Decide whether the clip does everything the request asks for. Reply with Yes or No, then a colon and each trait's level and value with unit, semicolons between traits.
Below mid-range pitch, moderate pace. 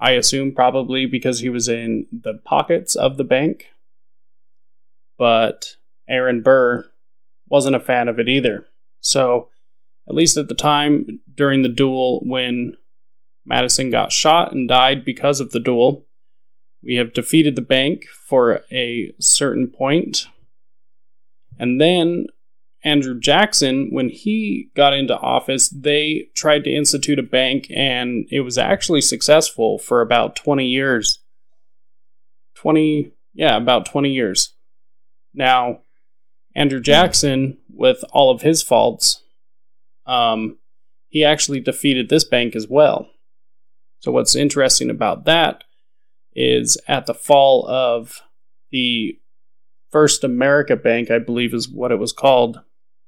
No: low, 130 Hz; slow, 130 wpm